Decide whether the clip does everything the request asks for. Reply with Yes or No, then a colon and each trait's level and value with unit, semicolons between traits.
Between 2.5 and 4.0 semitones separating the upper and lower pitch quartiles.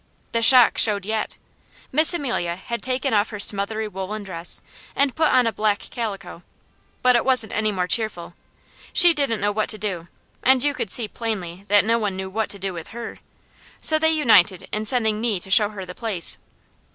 Yes: average, 3.6 semitones